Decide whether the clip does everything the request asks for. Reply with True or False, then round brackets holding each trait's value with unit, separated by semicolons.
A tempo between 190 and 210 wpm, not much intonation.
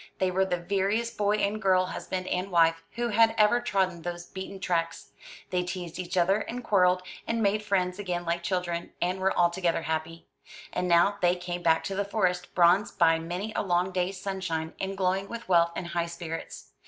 True (195 wpm; 2.3 semitones)